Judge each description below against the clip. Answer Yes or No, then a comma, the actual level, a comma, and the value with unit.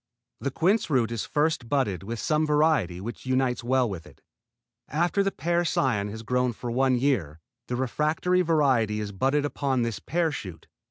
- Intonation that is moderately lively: Yes, average, 4.9 semitones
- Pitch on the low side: Yes, low, 130 Hz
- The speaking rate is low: No, average, 170 wpm